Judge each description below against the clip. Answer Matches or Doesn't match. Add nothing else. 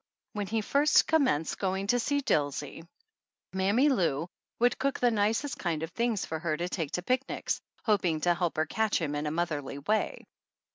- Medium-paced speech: Matches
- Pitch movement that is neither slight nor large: Doesn't match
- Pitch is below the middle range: Doesn't match